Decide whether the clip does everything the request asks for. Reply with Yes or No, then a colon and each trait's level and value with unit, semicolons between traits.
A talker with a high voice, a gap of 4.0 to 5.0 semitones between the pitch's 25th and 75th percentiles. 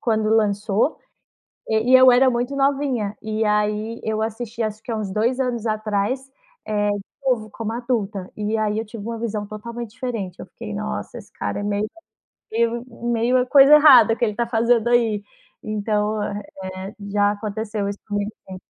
No: high, 220 Hz; narrow, 2.4 semitones